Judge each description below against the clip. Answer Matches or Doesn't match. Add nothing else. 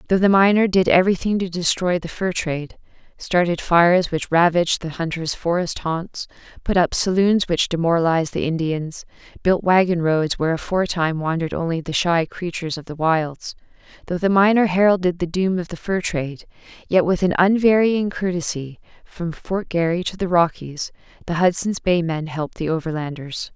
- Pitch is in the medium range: Matches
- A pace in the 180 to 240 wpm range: Doesn't match